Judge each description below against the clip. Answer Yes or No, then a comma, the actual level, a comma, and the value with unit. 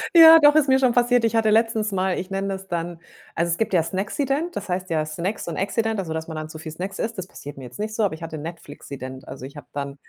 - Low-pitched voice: No, medium, 185 Hz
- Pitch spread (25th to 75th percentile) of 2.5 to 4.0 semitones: No, wide, 5.8 semitones